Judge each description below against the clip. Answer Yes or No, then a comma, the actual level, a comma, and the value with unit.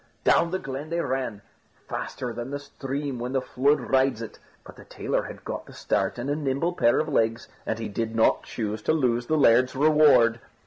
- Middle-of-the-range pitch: No, low, 130 Hz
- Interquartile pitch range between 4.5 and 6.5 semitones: No, average, 3.7 semitones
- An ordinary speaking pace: No, fast, 210 wpm